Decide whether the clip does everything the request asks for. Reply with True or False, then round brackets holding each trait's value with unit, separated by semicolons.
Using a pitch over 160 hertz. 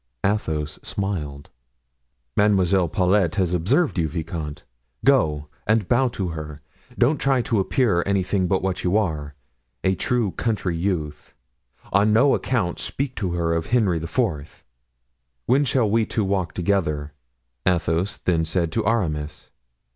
False (95 Hz)